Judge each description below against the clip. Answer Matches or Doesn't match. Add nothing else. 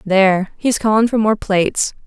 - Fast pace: Doesn't match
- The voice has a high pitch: Matches